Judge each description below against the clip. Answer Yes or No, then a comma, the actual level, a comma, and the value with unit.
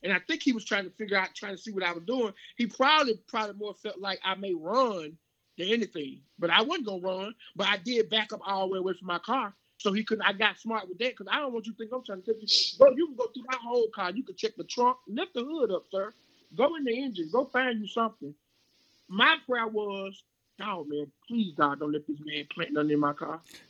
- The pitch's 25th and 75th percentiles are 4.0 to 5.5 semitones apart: Yes, average, 4.9 semitones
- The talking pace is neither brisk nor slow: No, fast, 270 wpm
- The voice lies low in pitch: No, high, 210 Hz